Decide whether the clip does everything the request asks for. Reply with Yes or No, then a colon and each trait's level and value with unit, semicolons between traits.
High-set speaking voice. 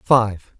No: low, 110 Hz